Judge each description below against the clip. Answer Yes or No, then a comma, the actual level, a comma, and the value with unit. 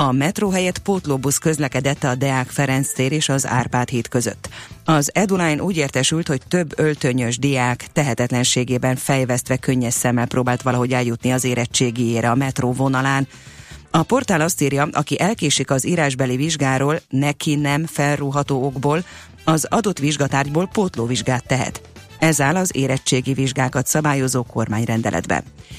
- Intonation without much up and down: No, average, 3.1 semitones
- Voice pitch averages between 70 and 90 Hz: No, low, 135 Hz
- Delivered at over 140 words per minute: No, average, 135 wpm